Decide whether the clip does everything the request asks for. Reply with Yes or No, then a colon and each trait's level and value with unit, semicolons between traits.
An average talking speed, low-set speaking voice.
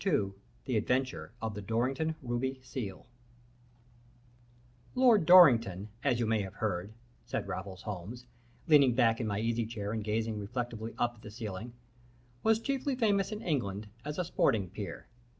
Yes: average, 155 wpm; low, 115 Hz